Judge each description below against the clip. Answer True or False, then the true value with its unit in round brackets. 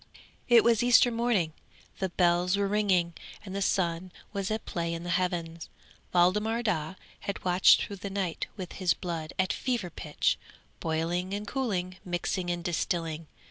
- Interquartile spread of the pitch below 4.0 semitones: True (2.8 semitones)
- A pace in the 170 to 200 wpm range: False (160 wpm)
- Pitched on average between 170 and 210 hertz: True (185 Hz)